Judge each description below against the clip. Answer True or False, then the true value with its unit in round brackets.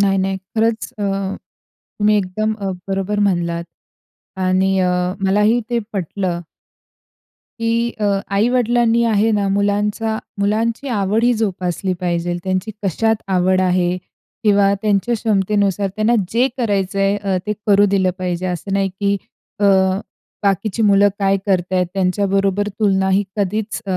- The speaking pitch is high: True (200 Hz)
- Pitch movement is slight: True (2.1 semitones)